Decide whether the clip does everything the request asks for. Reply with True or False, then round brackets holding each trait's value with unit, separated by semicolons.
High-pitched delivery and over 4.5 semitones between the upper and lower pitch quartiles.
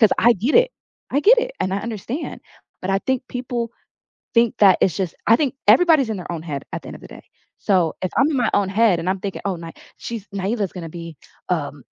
True (205 Hz; 5.2 semitones)